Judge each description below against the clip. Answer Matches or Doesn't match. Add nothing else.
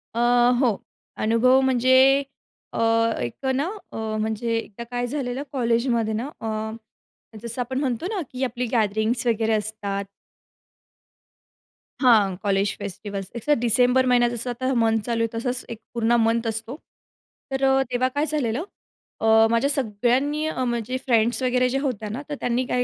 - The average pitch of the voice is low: Doesn't match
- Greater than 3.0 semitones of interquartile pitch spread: Doesn't match